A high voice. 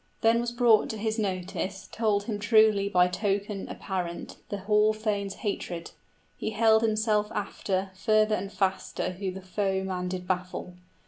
Yes: high, 205 Hz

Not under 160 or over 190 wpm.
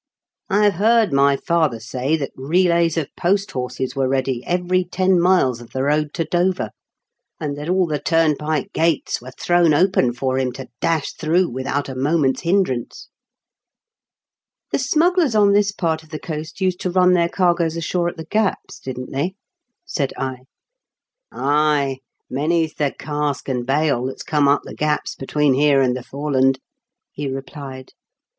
Yes: average, 170 wpm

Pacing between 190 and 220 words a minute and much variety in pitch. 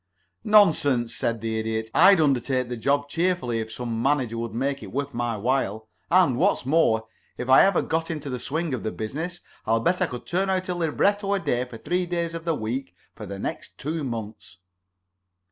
Yes: average, 200 wpm; wide, 6.5 semitones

